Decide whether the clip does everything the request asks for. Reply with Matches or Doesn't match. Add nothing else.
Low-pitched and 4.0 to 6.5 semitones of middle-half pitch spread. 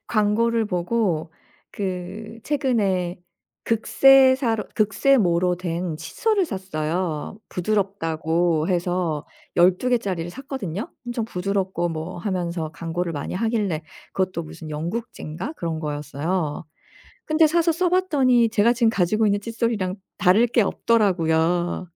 Doesn't match